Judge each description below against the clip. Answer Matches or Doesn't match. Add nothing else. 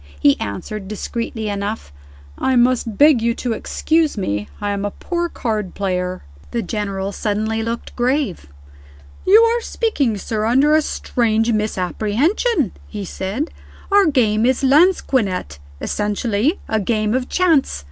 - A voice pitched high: Matches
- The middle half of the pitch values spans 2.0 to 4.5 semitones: Doesn't match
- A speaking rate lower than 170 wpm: Matches